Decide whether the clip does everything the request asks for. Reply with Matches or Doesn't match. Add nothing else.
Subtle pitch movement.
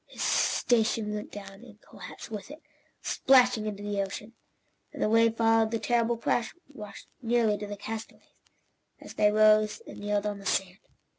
Matches